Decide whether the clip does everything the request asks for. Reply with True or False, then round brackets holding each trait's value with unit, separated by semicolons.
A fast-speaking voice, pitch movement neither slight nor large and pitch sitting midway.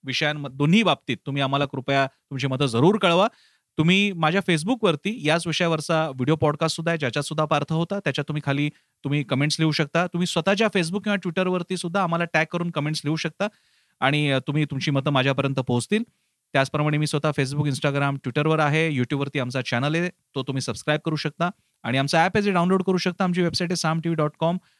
True (190 wpm; 3.7 semitones; 155 Hz)